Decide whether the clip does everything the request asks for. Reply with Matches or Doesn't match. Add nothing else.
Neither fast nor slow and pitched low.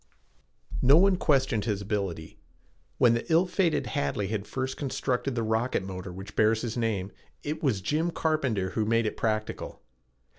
Matches